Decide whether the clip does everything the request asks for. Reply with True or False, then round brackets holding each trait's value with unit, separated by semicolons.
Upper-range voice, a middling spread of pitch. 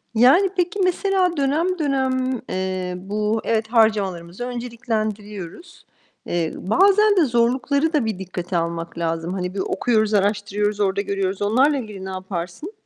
False (215 Hz; 6.2 semitones)